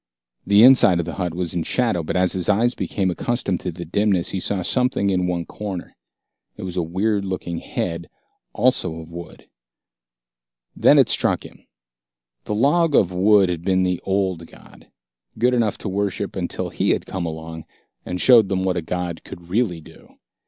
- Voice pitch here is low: Yes, very low, 95 Hz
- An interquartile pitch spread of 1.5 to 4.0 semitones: Yes, average, 2.9 semitones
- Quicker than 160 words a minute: Yes, average, 185 wpm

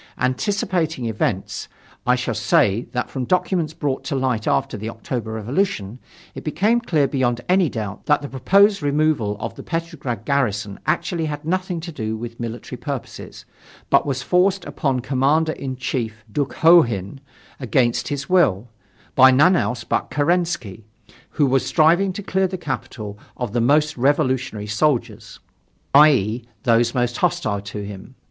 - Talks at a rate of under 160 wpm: Yes, average, 150 wpm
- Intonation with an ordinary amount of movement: No, wide, 5.7 semitones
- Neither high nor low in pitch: No, low, 130 Hz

